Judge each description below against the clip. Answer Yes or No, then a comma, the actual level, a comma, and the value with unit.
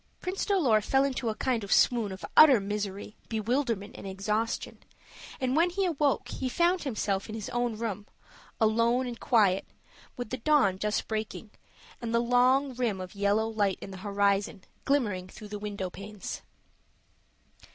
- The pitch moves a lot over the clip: No, average, 4.1 semitones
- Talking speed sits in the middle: Yes, average, 160 wpm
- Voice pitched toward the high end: Yes, high, 220 Hz